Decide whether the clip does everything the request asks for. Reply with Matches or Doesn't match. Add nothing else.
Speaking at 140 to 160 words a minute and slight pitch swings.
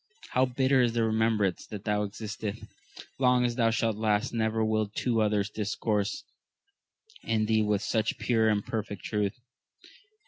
Matches